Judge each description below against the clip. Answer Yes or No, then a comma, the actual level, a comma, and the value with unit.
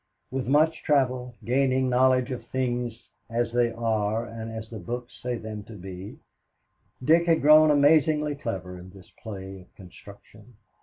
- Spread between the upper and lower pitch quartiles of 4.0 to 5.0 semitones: No, average, 3.5 semitones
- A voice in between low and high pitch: No, low, 120 Hz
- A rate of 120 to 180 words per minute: Yes, average, 155 wpm